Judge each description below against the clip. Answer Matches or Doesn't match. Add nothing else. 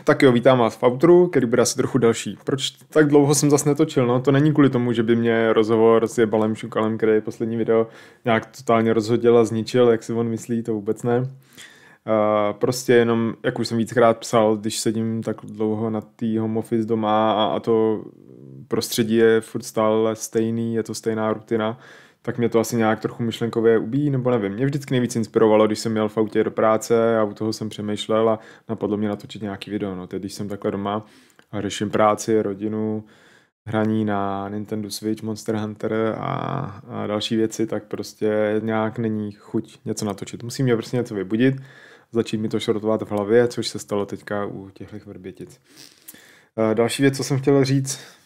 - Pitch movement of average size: Doesn't match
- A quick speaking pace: Matches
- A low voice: Matches